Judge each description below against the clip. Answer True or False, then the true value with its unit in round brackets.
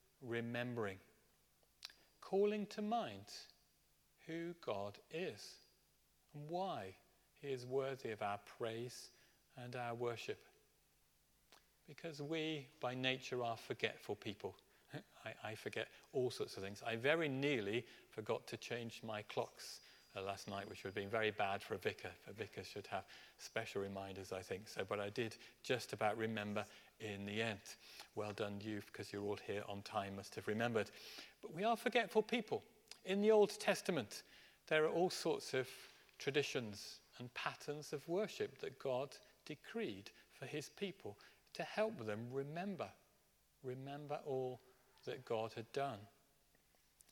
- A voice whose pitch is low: True (125 Hz)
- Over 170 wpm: False (150 wpm)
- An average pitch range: False (6.8 semitones)